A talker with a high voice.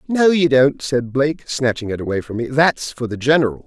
No: low, 135 Hz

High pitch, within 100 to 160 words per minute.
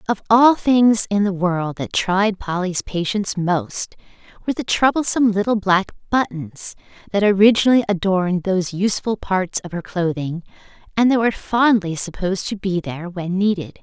Yes: high, 195 Hz; average, 155 wpm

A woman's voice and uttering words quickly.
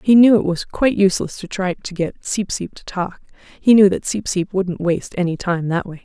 Yes: female; fast, 250 wpm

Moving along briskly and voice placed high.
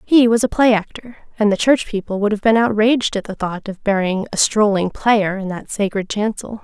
Yes: fast, 225 wpm; high, 210 Hz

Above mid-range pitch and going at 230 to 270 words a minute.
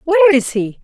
No: very high, 290 Hz; fast, 215 wpm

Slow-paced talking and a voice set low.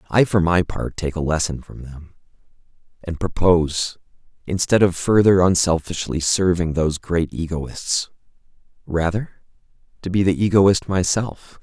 Yes: slow, 130 wpm; very low, 90 Hz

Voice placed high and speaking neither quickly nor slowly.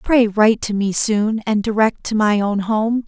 No: high, 215 Hz; fast, 215 wpm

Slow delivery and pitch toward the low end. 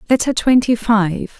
No: slow, 130 wpm; high, 225 Hz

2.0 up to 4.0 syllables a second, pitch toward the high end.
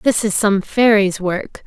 Yes: 3.7 syllables/s; high, 205 Hz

